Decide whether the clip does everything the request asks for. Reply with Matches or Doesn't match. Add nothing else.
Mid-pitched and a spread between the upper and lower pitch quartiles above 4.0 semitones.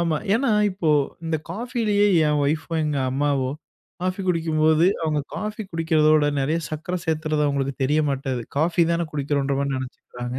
Doesn't match